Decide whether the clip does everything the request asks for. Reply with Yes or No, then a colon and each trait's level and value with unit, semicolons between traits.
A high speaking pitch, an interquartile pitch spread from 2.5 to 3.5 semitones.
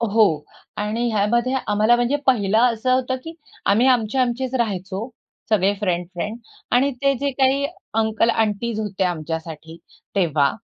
No: high, 220 Hz; average, 4.0 semitones